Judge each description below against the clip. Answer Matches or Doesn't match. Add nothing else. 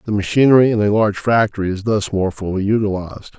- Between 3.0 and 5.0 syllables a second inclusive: Doesn't match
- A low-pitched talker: Matches